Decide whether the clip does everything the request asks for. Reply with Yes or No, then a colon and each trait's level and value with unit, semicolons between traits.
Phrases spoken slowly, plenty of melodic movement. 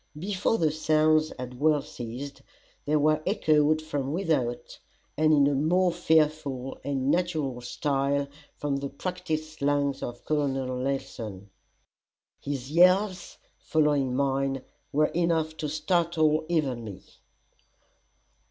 No: slow, 115 wpm; narrow, 2.6 semitones